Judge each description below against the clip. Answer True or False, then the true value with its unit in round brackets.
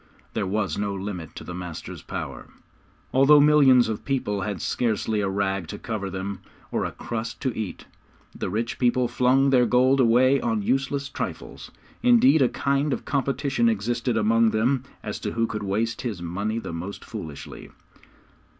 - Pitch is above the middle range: False (115 Hz)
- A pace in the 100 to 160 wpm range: False (170 wpm)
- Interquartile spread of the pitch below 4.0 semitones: False (4.5 semitones)